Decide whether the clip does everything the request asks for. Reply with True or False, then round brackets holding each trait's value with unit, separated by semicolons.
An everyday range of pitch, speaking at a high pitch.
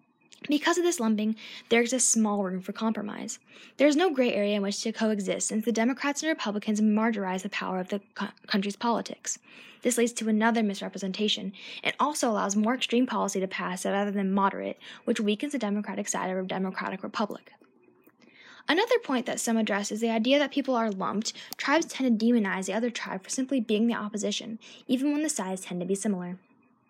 True (3.5 semitones; 225 Hz)